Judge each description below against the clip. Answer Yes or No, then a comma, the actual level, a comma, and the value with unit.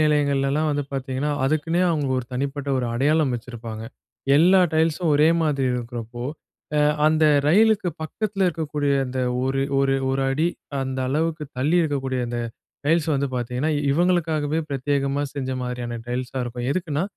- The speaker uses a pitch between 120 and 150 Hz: Yes, medium, 140 Hz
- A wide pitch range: No, average, 3.3 semitones